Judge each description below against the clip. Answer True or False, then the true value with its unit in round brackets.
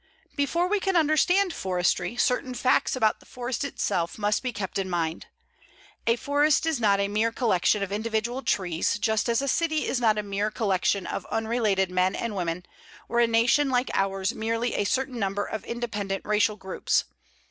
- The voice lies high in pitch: True (220 Hz)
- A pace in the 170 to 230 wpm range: True (180 wpm)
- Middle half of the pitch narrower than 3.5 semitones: False (4.2 semitones)